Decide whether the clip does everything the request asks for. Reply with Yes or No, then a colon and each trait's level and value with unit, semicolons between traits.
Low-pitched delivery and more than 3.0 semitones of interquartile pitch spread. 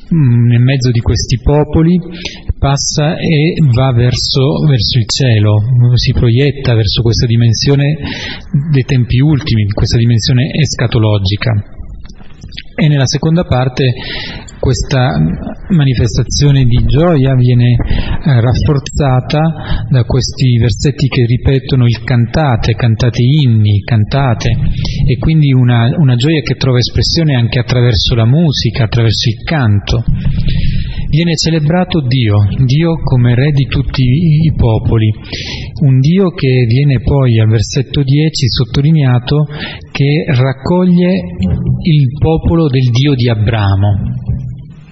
Yes: low, 130 Hz; average, 3.6 semitones